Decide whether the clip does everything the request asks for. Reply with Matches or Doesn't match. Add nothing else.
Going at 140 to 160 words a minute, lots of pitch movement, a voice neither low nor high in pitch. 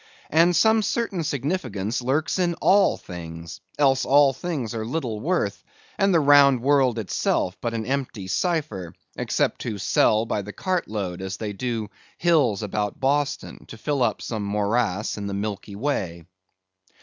Doesn't match